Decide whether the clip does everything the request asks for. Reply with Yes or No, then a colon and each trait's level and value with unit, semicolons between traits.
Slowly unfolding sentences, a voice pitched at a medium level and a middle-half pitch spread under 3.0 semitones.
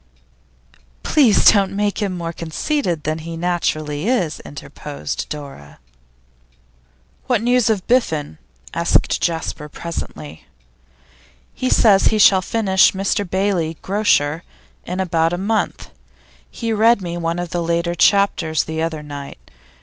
No: slow, 125 wpm; medium, 175 Hz; average, 4.3 semitones